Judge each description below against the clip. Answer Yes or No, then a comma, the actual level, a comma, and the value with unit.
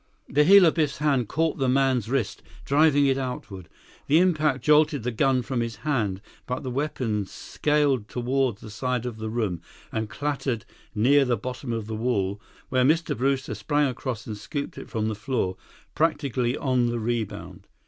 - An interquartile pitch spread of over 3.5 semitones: Yes, average, 4.1 semitones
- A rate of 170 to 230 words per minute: Yes, average, 180 wpm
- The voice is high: No, low, 130 Hz